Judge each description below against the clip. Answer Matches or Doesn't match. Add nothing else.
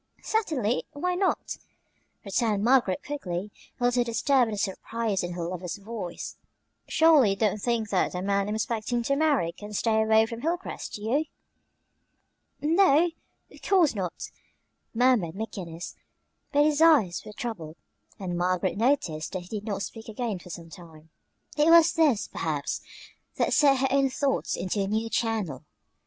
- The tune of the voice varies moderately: Doesn't match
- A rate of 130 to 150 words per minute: Doesn't match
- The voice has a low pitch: Doesn't match